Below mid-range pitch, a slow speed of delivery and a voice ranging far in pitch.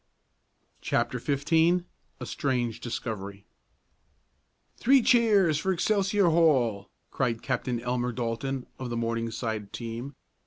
Yes: low, 125 Hz; slow, 105 wpm; wide, 6.2 semitones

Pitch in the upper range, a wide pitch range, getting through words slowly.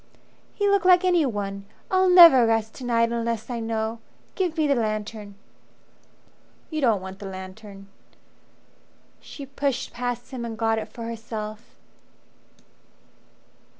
No: high, 230 Hz; average, 4.3 semitones; slow, 130 wpm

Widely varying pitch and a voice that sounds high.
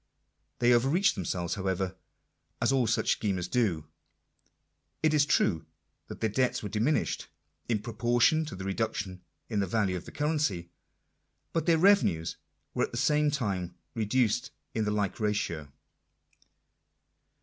No: wide, 5.7 semitones; low, 110 Hz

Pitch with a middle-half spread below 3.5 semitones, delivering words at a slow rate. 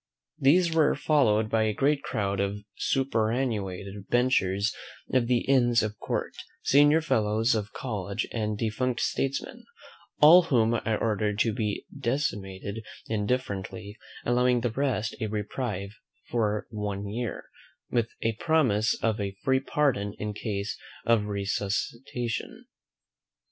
No: average, 3.8 semitones; slow, 125 wpm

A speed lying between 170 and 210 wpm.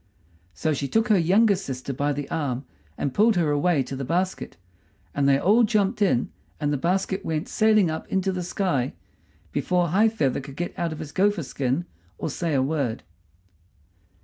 Yes: average, 185 wpm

